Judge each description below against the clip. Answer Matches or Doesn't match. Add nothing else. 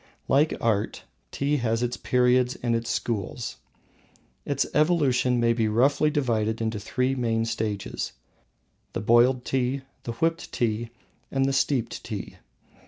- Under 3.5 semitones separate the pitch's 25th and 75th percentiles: Matches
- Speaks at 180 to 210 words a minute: Doesn't match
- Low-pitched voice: Matches